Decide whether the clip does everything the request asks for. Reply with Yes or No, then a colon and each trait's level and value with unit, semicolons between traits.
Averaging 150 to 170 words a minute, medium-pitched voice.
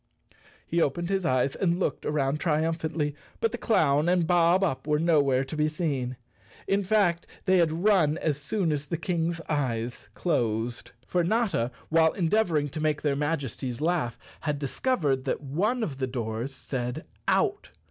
Yes: average, 165 wpm; medium, 155 Hz